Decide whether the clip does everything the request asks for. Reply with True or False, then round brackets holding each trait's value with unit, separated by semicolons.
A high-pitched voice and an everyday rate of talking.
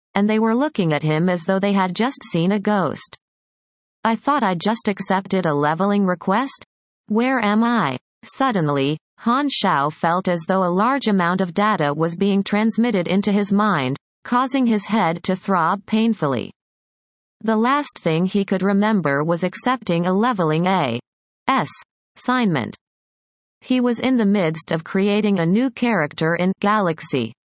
True (200 Hz; 160 wpm)